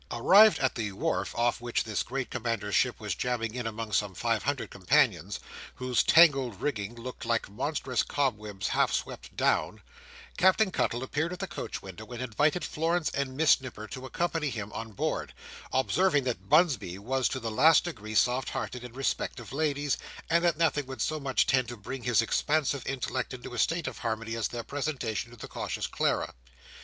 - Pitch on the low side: Yes, low, 125 Hz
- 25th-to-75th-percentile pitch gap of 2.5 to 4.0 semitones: No, average, 4.4 semitones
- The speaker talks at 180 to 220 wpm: Yes, average, 190 wpm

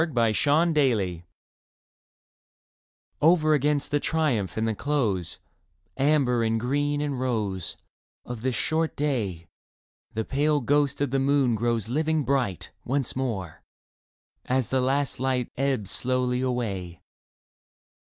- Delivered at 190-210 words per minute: No, slow, 135 wpm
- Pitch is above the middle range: No, low, 130 Hz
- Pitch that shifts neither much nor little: Yes, average, 4.2 semitones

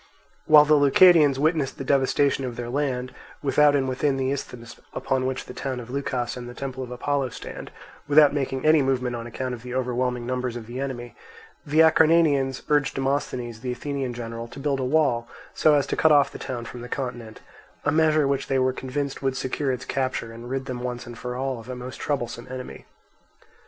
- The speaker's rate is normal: No, fast, 210 wpm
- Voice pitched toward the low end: Yes, low, 130 Hz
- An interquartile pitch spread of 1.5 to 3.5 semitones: Yes, narrow, 2.4 semitones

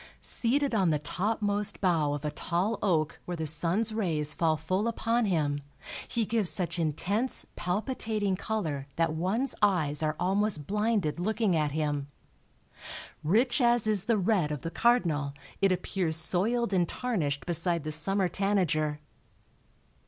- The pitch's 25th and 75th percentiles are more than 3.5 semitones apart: Yes, wide, 5.6 semitones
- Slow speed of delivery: No, average, 145 wpm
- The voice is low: No, medium, 180 Hz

